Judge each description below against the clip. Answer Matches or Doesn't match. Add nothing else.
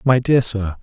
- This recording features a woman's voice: Doesn't match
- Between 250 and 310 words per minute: Doesn't match